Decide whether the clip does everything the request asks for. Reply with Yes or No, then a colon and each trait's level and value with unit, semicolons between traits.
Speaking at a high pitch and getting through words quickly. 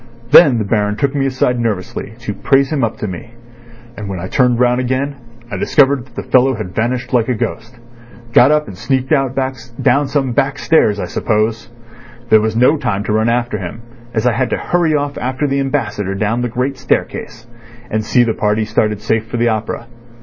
No: low, 120 Hz; fast, 210 wpm